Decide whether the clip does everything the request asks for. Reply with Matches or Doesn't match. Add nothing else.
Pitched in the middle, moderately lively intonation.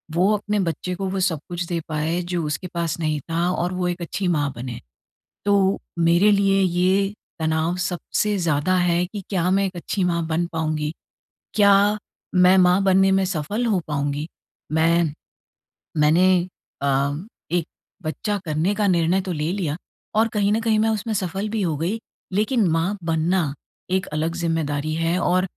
Matches